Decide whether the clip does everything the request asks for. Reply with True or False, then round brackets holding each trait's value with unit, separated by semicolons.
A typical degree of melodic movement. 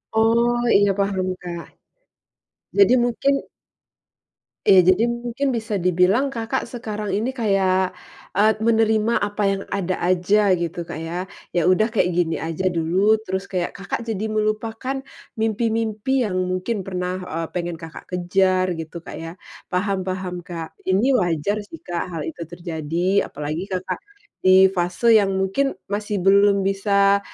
True (3.4 semitones)